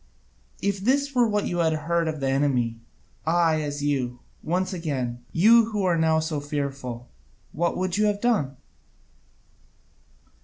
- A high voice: No, medium, 160 Hz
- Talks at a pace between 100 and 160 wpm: Yes, average, 150 wpm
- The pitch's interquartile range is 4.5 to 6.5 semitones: Yes, average, 5.1 semitones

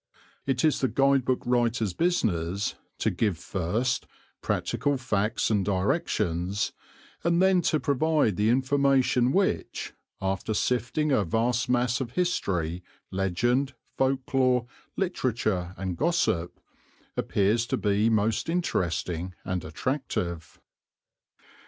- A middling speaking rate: No, slow, 115 wpm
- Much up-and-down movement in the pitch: Yes, wide, 5.9 semitones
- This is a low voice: Yes, low, 120 Hz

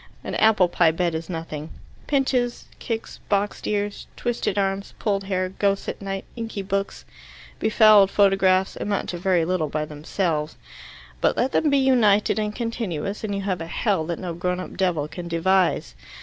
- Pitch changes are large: No, average, 3.4 semitones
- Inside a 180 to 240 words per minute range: No, average, 170 wpm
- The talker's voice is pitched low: No, high, 195 Hz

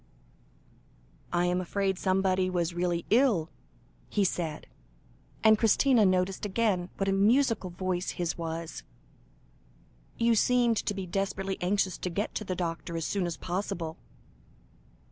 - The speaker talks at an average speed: No, slow, 130 wpm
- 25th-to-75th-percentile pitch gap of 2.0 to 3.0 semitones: Yes, average, 2.7 semitones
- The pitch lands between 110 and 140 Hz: No, medium, 185 Hz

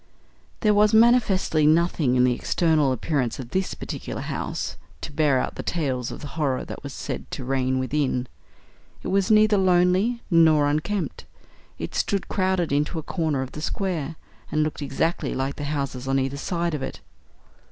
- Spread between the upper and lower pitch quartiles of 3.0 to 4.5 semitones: No, average, 5.2 semitones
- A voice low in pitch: No, medium, 155 Hz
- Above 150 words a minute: Yes, average, 175 wpm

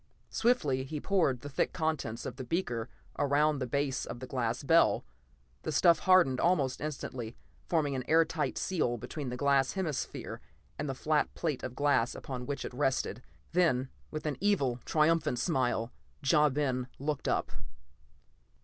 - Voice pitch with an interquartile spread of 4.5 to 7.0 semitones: No, average, 3.6 semitones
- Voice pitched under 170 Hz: Yes, medium, 140 Hz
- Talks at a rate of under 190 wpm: Yes, average, 160 wpm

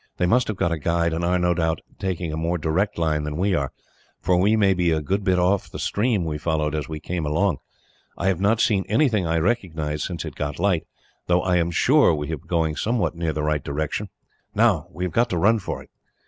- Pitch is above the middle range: No, very low, 85 Hz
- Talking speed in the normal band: No, fast, 245 wpm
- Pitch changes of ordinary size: Yes, average, 3.6 semitones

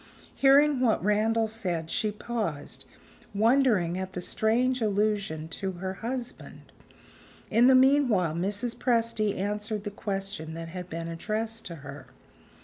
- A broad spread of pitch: No, average, 4.4 semitones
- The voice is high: Yes, high, 210 Hz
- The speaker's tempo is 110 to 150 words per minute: Yes, slow, 135 wpm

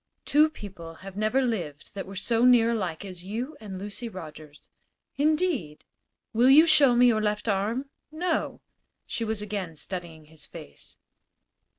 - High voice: Yes, high, 210 Hz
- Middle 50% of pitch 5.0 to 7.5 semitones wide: Yes, wide, 5.5 semitones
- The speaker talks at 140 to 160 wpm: Yes, average, 155 wpm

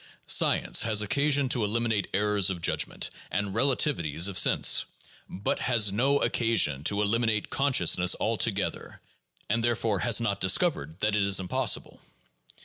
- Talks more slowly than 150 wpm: Yes, average, 140 wpm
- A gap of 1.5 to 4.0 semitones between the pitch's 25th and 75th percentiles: Yes, average, 3.3 semitones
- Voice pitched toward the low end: Yes, low, 105 Hz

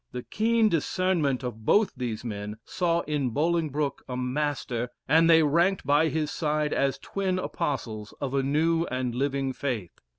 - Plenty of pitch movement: No, average, 4.7 semitones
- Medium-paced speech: Yes, average, 160 wpm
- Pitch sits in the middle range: Yes, medium, 145 Hz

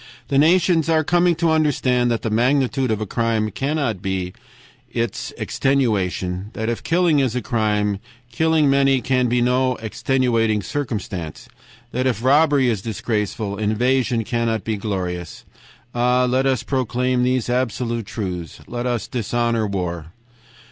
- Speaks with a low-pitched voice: Yes, low, 120 Hz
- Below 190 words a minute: Yes, average, 140 wpm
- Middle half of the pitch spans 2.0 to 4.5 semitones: Yes, average, 3.7 semitones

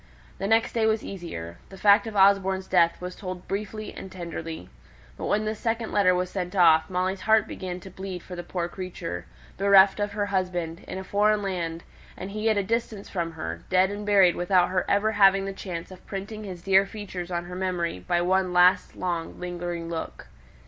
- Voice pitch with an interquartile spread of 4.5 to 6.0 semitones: No, narrow, 2.4 semitones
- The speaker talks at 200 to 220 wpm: Yes, fast, 205 wpm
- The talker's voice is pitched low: No, medium, 185 Hz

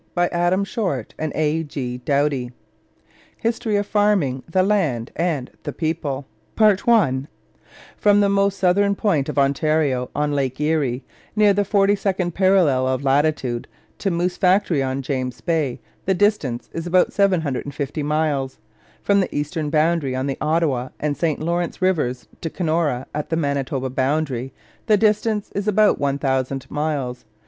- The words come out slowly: No, average, 145 wpm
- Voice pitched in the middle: Yes, medium, 155 Hz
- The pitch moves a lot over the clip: Yes, wide, 5.7 semitones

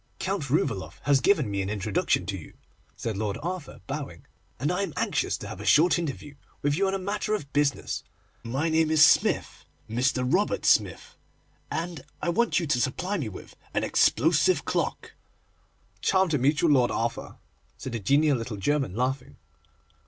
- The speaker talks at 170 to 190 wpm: Yes, average, 175 wpm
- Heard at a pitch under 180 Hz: Yes, medium, 140 Hz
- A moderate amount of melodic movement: No, wide, 6.2 semitones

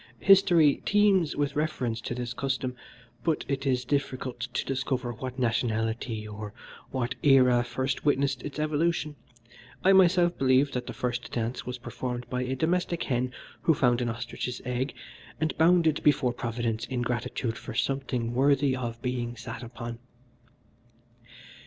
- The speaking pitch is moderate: No, low, 130 Hz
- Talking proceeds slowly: No, average, 145 wpm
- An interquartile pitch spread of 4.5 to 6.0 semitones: No, average, 3.2 semitones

